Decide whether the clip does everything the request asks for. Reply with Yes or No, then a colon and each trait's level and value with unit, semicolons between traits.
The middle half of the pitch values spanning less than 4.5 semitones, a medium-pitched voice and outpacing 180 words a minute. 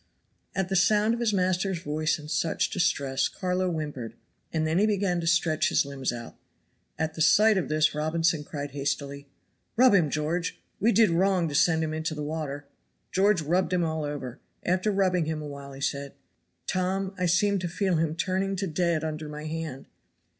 Yes: average, 3.7 semitones; medium, 165 Hz; average, 190 wpm